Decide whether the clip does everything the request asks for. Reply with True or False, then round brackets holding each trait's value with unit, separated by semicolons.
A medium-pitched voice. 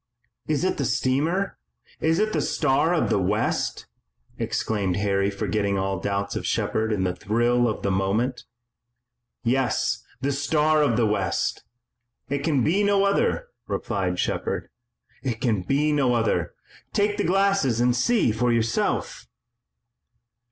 False (120 Hz)